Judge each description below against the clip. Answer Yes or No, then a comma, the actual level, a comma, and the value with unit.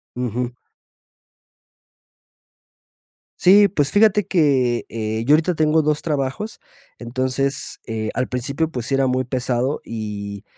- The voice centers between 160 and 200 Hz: No, low, 130 Hz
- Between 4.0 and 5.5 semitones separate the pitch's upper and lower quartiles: Yes, average, 4.3 semitones